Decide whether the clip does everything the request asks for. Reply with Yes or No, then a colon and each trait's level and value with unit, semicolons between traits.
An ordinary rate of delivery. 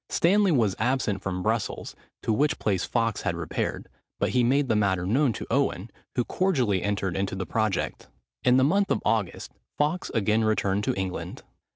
Yes: average, 180 wpm